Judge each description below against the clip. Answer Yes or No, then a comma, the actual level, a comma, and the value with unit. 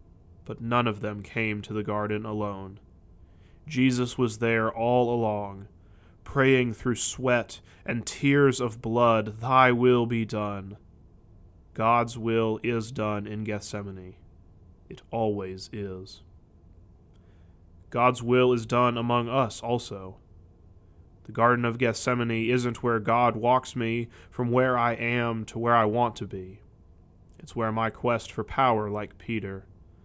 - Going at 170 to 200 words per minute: No, slow, 135 wpm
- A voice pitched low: Yes, low, 110 Hz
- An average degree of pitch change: Yes, average, 4.1 semitones